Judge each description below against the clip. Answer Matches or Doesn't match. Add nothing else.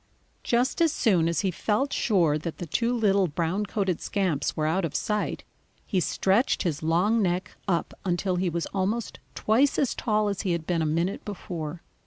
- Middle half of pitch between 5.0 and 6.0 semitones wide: Doesn't match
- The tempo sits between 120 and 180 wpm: Doesn't match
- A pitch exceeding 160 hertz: Matches